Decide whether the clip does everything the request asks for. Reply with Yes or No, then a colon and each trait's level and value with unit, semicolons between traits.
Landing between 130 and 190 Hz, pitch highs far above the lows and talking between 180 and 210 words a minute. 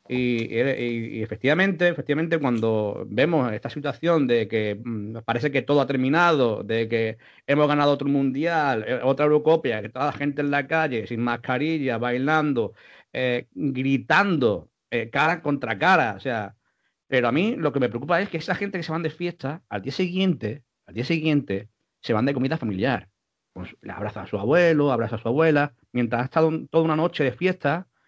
No: medium, 140 Hz; average, 5.0 semitones; fast, 190 wpm